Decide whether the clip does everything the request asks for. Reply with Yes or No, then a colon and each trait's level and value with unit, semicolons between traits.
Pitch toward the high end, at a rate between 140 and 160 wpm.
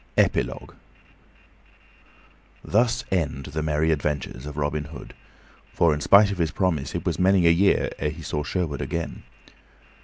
No: very low, 80 Hz; average, 150 wpm